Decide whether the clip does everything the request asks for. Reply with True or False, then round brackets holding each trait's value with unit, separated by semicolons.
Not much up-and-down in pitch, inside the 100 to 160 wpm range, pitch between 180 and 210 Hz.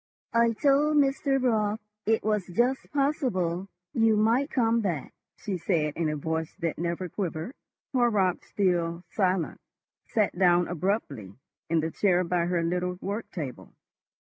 False (5.1 semitones; 140 wpm; 190 Hz)